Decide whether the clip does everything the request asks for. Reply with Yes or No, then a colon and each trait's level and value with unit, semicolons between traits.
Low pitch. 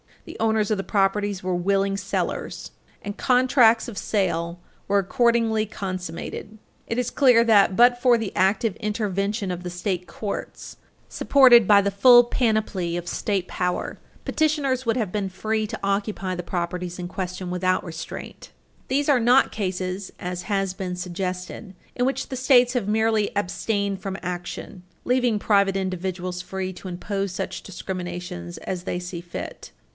No: high, 195 Hz